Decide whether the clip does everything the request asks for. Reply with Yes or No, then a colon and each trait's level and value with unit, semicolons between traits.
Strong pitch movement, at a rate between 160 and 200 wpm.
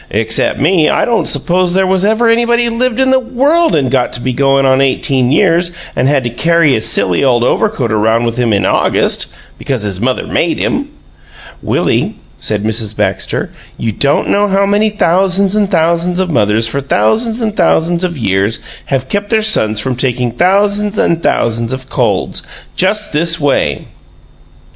Yes: wide, 9.0 semitones; average, 180 wpm